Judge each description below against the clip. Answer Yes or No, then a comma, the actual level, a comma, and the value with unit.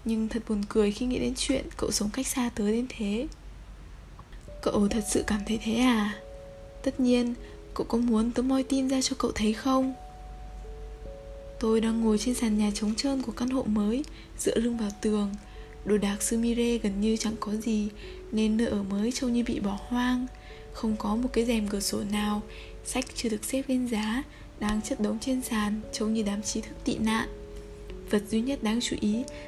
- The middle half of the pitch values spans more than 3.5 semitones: No, average, 2.8 semitones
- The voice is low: No, high, 225 Hz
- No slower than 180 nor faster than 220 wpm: Yes, average, 205 wpm